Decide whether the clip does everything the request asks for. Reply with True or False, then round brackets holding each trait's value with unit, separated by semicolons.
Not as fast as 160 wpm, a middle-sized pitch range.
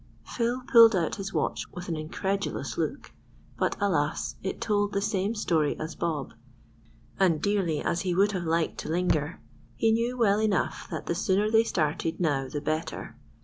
False (175 wpm; 4.4 semitones)